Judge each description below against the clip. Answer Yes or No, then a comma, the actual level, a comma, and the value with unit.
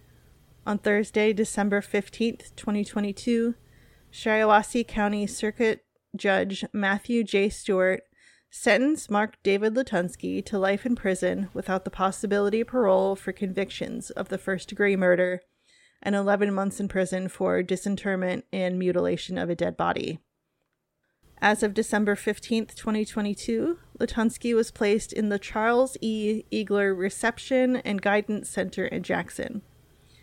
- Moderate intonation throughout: No, narrow, 2.3 semitones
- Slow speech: Yes, slow, 125 wpm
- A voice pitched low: No, high, 205 Hz